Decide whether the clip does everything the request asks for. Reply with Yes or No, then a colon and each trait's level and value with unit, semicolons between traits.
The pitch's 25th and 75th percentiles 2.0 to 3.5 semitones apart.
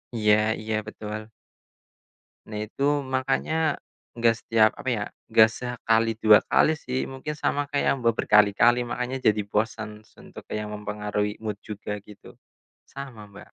Yes: narrow, 2.6 semitones